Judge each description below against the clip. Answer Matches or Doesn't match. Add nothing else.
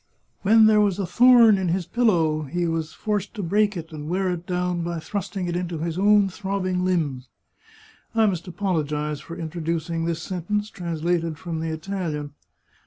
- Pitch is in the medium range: Matches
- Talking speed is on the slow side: Doesn't match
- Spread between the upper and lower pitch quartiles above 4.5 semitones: Doesn't match